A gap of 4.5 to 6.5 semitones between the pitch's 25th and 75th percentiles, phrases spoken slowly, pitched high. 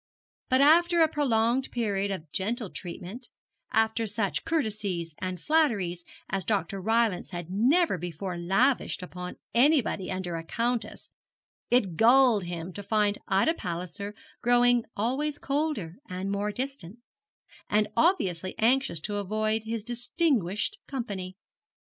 Yes: average, 5.0 semitones; slow, 125 wpm; high, 215 Hz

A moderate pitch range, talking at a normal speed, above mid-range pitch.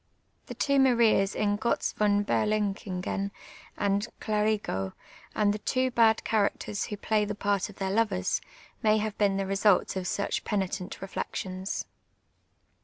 No: narrow, 1.8 semitones; average, 145 wpm; high, 205 Hz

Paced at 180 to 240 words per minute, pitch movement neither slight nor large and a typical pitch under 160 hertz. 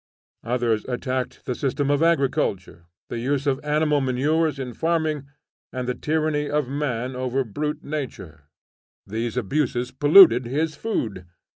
No: slow, 135 wpm; average, 3.5 semitones; low, 135 Hz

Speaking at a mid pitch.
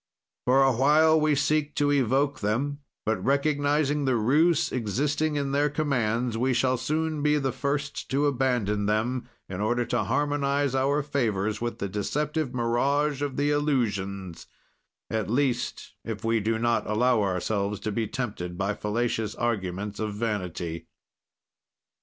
No: low, 125 Hz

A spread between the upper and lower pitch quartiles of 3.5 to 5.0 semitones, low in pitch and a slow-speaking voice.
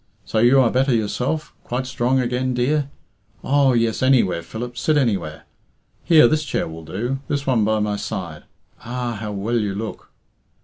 No: average, 3.8 semitones; low, 120 Hz; average, 175 wpm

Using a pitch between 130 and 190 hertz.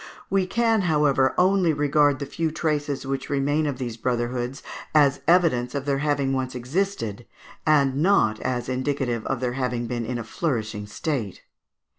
Yes: low, 135 Hz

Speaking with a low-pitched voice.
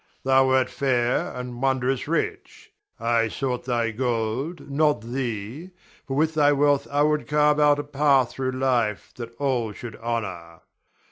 Yes: low, 130 Hz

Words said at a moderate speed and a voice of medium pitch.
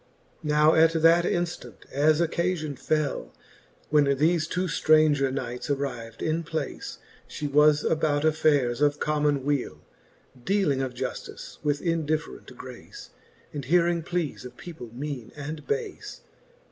No: slow, 130 wpm; medium, 150 Hz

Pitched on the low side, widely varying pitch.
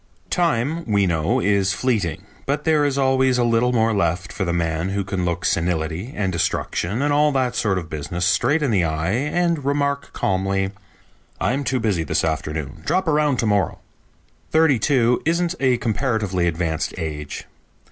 Yes: low, 110 Hz; wide, 7.9 semitones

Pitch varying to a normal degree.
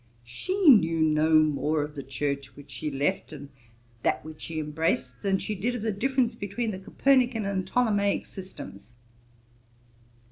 No: wide, 6.6 semitones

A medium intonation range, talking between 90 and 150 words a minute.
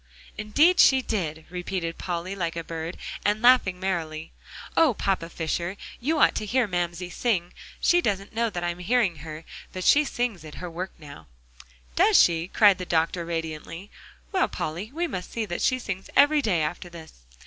No: average, 4.9 semitones; average, 175 wpm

